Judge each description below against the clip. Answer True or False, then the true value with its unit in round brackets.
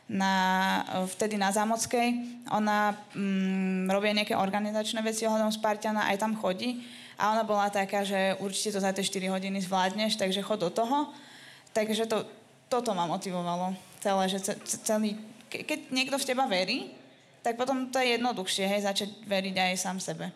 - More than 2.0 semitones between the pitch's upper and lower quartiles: True (2.7 semitones)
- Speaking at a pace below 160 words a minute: False (165 wpm)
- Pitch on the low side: False (210 Hz)